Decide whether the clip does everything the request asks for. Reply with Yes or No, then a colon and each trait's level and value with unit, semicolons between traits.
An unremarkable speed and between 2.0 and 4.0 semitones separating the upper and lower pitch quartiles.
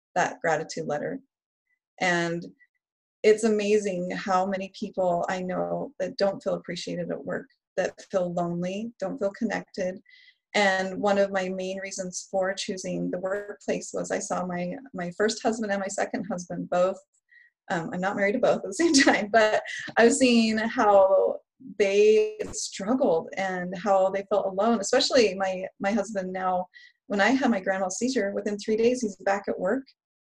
Yes: average, 165 wpm; average, 3.7 semitones